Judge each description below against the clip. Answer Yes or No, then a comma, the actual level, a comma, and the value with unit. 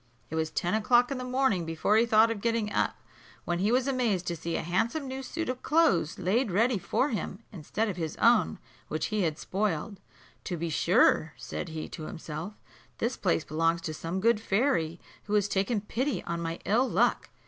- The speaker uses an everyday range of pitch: No, wide, 5.8 semitones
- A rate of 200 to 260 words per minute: Yes, fast, 205 wpm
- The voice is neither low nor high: No, high, 205 Hz